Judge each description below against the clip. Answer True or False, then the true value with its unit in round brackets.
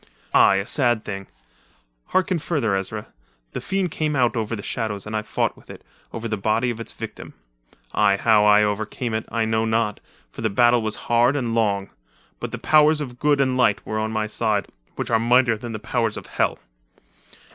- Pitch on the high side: False (115 Hz)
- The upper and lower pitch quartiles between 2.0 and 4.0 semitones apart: True (2.5 semitones)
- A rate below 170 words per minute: False (200 wpm)